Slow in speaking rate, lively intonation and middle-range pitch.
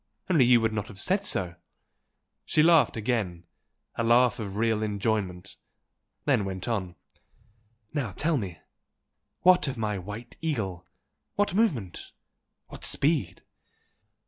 No: slow, 125 wpm; wide, 6.1 semitones; low, 110 Hz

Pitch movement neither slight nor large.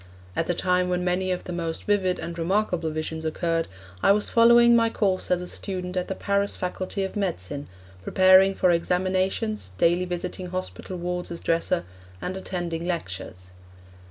No: narrow, 2.1 semitones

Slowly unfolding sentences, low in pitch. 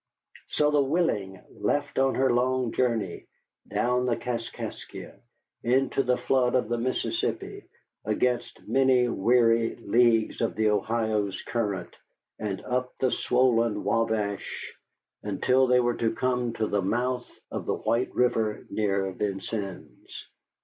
Yes: slow, 130 wpm; low, 120 Hz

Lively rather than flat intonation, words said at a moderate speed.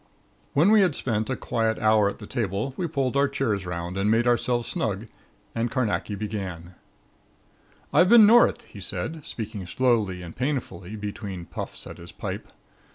No: average, 5.0 semitones; average, 165 wpm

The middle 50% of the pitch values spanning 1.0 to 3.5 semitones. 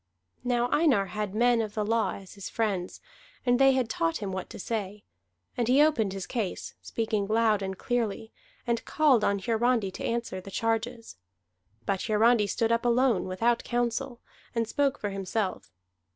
Yes: average, 3.2 semitones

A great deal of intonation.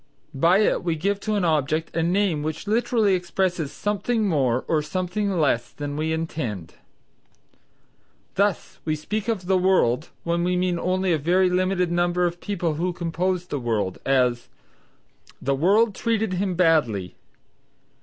No: average, 3.7 semitones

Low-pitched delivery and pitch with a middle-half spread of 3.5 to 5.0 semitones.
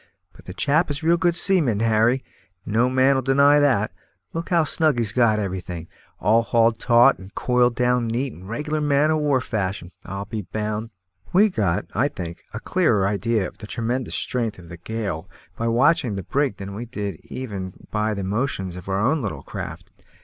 No: low, 115 Hz; wide, 5.4 semitones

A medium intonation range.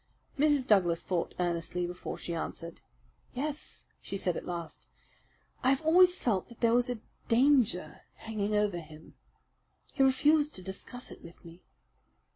No: wide, 7.3 semitones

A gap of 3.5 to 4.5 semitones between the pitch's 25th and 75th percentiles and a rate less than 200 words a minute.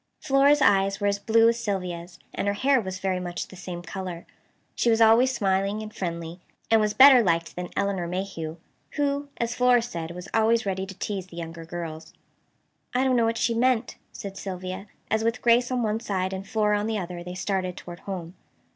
No: average, 4.2 semitones; fast, 205 wpm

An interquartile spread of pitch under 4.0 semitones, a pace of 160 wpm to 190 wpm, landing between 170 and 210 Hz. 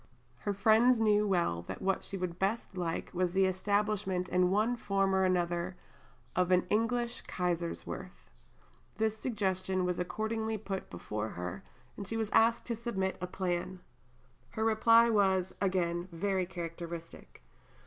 No: average, 3.3 semitones; average, 145 wpm; high, 190 Hz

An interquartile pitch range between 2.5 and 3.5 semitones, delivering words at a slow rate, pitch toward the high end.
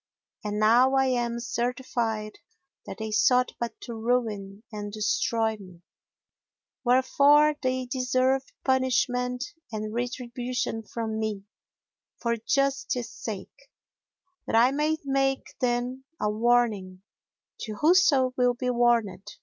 Yes: average, 2.9 semitones; slow, 115 wpm; high, 240 Hz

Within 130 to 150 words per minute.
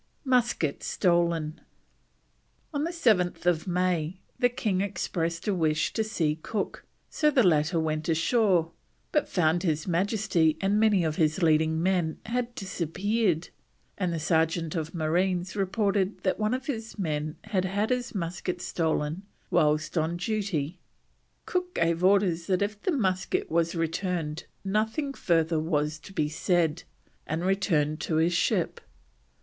Yes: average, 140 wpm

